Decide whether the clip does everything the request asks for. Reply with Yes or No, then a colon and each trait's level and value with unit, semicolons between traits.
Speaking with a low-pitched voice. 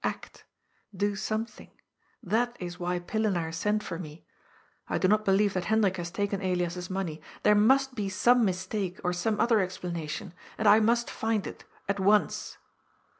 No: high, 195 Hz